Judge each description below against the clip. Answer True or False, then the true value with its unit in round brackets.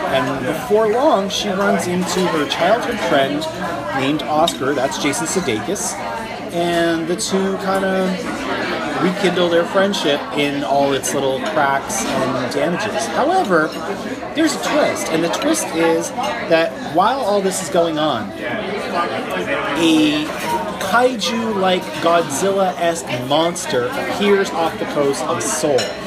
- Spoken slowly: True (130 wpm)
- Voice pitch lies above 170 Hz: True (185 Hz)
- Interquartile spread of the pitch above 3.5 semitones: False (3.2 semitones)